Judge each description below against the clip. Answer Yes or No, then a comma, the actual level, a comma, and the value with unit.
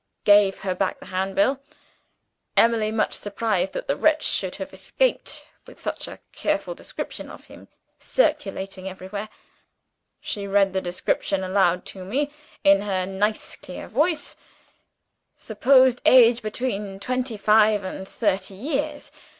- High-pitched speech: Yes, high, 205 Hz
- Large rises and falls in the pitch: No, average, 4.3 semitones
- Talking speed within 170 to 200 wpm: No, slow, 135 wpm